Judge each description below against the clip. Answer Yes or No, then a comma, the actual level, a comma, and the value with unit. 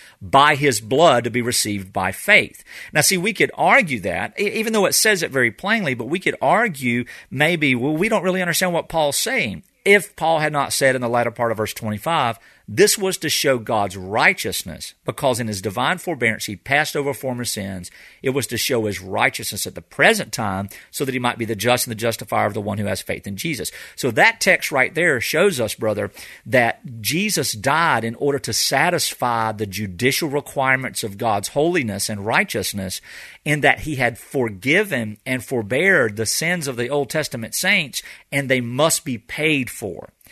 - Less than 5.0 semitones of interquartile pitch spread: No, average, 5.3 semitones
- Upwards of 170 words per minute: Yes, average, 200 wpm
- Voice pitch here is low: Yes, low, 125 Hz